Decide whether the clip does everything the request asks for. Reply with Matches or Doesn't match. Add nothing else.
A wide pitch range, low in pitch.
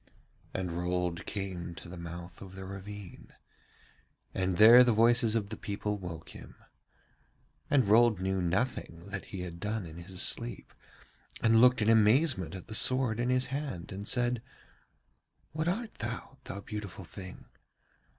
Doesn't match